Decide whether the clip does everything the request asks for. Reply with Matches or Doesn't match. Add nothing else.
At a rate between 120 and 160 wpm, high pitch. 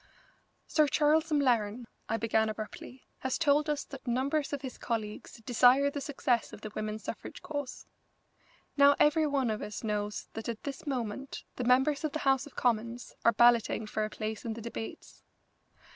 Doesn't match